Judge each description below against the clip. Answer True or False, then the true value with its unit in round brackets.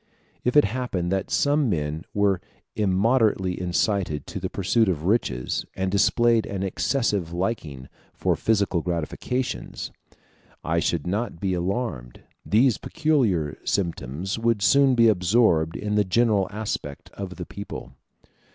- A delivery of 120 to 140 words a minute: True (135 wpm)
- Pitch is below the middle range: True (100 Hz)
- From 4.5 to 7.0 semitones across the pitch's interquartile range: True (4.9 semitones)